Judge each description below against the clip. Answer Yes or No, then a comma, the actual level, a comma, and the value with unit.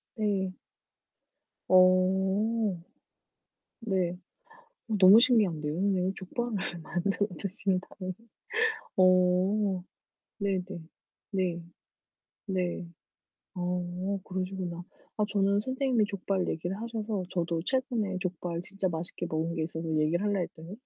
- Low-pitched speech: No, medium, 185 Hz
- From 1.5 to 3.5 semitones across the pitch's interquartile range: Yes, narrow, 2.4 semitones